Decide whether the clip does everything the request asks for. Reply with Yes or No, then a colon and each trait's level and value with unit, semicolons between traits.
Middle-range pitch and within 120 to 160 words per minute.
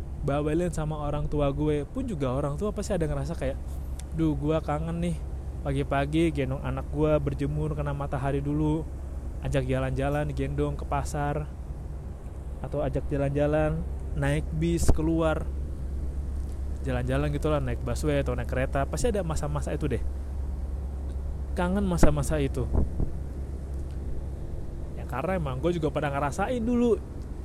No: very low, 75 Hz; average, 130 wpm